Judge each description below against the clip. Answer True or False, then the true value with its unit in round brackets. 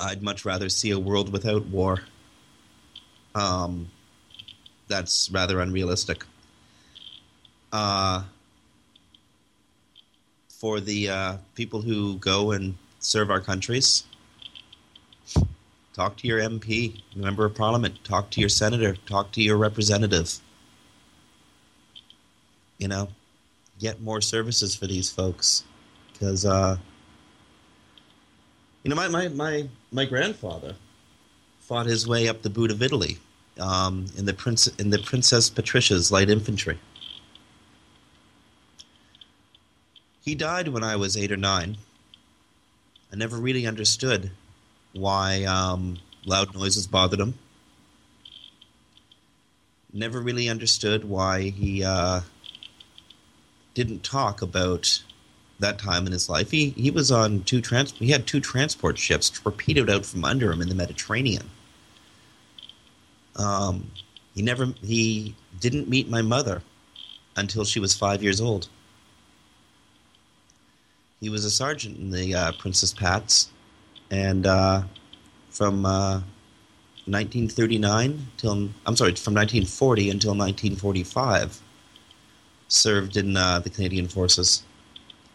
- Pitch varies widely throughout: False (2.8 semitones)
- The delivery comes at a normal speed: False (115 wpm)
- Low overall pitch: True (100 Hz)